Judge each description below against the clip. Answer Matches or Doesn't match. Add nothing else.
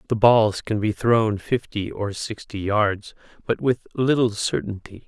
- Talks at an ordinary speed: Matches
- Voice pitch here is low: Matches